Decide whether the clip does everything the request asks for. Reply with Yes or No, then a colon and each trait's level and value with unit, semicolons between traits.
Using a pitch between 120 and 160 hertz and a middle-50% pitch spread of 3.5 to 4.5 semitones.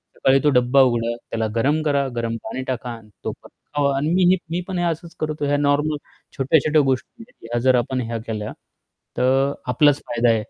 Yes: low, 135 Hz; average, 3.8 semitones